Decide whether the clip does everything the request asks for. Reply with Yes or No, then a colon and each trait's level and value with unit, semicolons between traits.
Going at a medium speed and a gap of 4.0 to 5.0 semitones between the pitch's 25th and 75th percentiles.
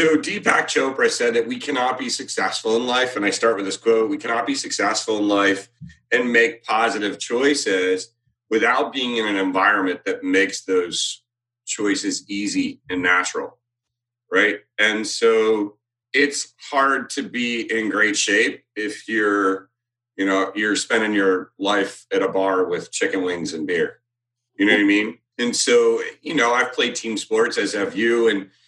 Yes: average, 170 wpm; average, 4.4 semitones